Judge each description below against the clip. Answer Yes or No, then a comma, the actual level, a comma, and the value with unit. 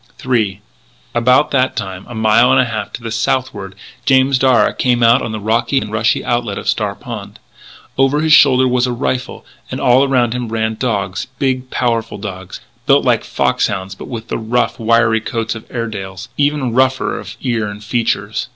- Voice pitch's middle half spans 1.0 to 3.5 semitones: Yes, average, 2.8 semitones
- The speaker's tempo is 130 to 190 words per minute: Yes, average, 185 wpm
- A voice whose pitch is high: No, low, 115 Hz